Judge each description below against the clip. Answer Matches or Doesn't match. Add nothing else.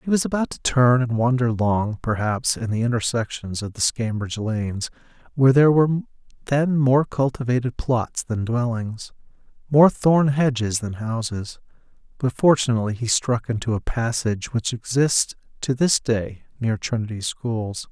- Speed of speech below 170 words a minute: Matches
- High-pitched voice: Doesn't match